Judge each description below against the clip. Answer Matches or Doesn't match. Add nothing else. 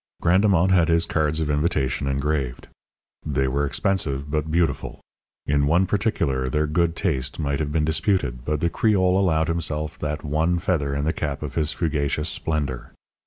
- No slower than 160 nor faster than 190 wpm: Matches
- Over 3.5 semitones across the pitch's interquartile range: Doesn't match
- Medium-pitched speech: Doesn't match